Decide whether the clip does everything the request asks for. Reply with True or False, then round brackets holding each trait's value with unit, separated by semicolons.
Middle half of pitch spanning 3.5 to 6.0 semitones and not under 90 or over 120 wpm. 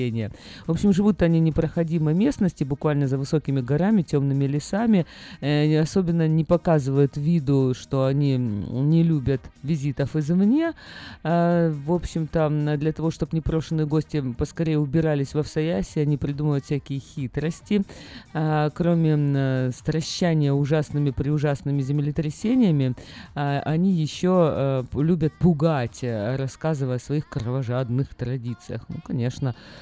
False (3.0 semitones; 110 wpm)